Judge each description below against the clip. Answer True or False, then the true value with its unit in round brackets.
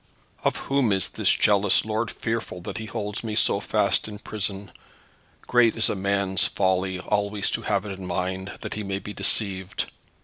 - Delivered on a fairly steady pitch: True (2.0 semitones)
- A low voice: True (100 Hz)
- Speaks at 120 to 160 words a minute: False (180 wpm)